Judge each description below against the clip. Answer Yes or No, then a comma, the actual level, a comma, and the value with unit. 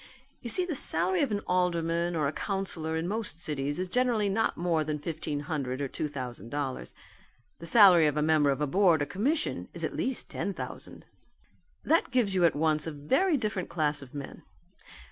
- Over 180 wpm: Yes, average, 195 wpm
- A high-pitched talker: No, medium, 165 Hz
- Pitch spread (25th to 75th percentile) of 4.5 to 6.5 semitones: Yes, average, 5.3 semitones